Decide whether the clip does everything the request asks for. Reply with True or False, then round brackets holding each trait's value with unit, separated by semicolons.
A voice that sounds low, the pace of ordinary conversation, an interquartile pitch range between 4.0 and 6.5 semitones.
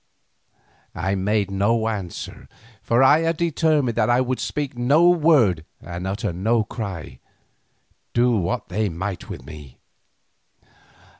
False (110 Hz; 130 wpm; 5.6 semitones)